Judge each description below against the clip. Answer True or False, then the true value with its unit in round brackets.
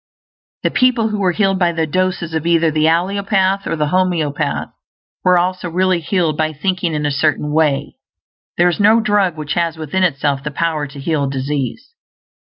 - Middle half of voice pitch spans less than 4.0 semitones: True (3.6 semitones)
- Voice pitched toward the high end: False (170 Hz)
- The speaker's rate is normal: True (180 wpm)